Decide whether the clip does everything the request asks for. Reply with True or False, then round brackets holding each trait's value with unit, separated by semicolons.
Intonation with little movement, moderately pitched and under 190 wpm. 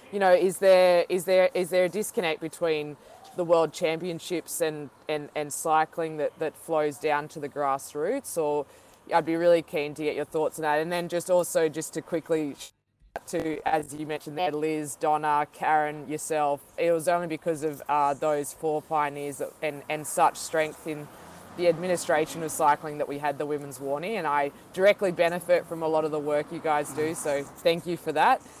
False (2.3 semitones; 155 Hz; 200 wpm)